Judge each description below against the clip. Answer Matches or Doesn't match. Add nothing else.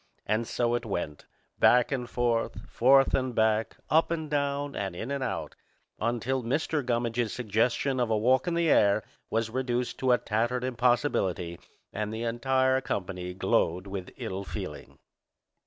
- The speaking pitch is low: Matches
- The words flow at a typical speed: Matches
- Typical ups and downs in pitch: Matches